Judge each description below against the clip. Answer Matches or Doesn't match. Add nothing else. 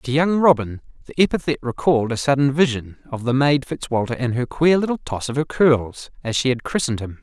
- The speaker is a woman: Doesn't match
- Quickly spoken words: Matches